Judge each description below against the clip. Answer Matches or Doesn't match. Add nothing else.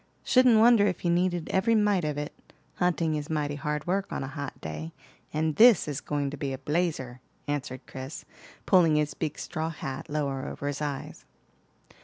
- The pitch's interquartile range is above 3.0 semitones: Matches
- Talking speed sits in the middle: Matches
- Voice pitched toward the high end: Doesn't match